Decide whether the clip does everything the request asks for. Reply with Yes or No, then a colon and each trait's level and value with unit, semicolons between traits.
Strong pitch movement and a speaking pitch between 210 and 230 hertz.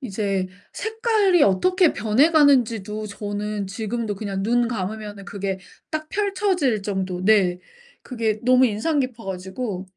Yes: wide, 5.8 semitones; high, 220 Hz